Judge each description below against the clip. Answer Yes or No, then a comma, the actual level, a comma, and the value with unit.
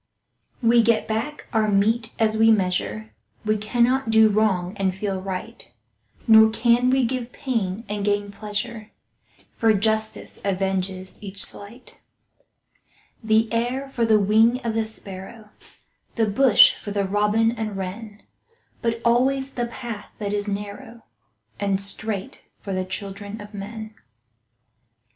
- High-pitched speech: Yes, high, 215 Hz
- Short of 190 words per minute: Yes, slow, 135 wpm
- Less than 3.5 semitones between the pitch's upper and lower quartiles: Yes, narrow, 2.4 semitones